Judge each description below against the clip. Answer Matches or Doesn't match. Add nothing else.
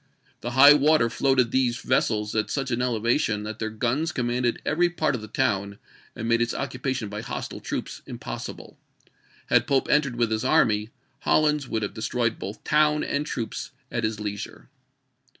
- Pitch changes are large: Doesn't match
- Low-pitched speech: Matches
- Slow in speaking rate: Doesn't match